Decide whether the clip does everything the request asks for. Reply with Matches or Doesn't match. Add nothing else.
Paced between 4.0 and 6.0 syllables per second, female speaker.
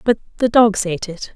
Matches